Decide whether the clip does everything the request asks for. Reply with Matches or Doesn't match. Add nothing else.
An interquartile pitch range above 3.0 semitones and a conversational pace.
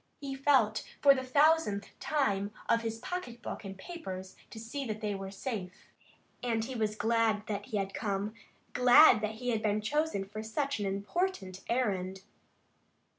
Matches